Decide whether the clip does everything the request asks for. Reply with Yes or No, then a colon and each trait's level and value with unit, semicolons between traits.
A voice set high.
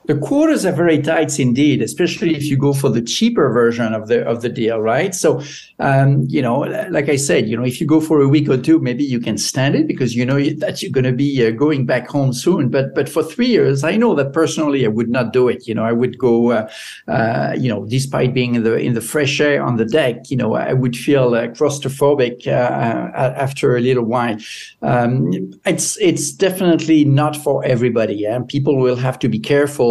No: low, 135 Hz